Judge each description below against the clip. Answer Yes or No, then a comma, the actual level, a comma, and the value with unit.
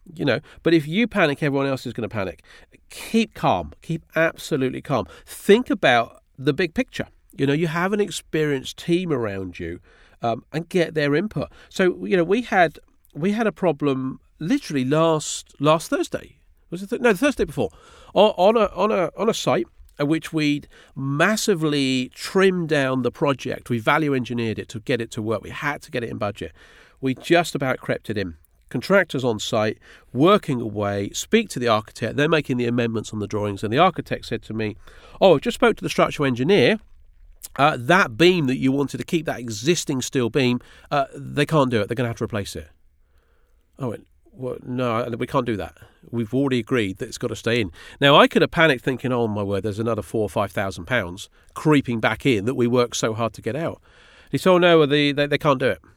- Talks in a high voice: No, low, 135 Hz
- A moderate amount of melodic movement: No, wide, 6.0 semitones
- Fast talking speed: Yes, fast, 215 wpm